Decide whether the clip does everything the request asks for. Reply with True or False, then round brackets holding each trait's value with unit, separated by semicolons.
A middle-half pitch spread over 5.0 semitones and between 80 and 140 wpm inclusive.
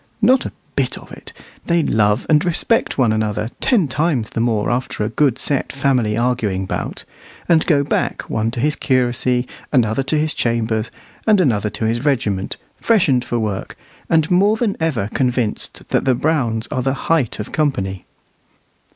False (5.6 semitones; 170 wpm)